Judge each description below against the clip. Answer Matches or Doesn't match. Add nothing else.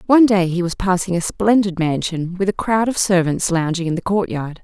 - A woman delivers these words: Matches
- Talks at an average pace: Doesn't match